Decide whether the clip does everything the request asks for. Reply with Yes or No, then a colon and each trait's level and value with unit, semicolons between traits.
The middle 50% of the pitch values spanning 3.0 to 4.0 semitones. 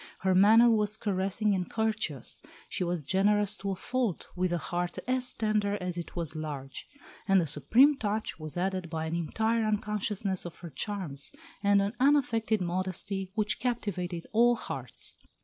Yes: average, 3.7 semitones